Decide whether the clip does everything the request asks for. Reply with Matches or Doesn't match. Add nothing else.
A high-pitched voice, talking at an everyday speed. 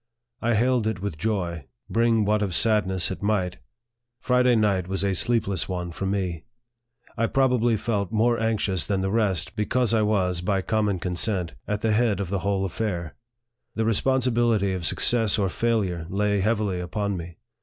Doesn't match